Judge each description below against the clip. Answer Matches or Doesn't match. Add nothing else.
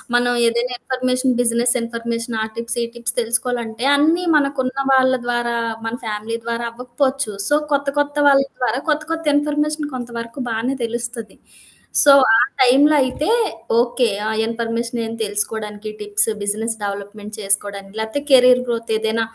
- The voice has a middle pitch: Doesn't match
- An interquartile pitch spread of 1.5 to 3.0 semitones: Matches